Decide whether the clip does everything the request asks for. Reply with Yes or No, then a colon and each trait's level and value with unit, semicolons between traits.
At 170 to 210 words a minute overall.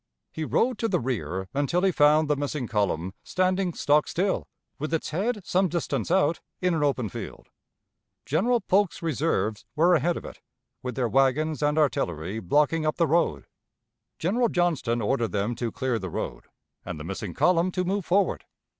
Yes: average, 175 wpm